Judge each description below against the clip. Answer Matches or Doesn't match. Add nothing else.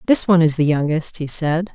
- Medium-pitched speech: Matches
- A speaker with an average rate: Doesn't match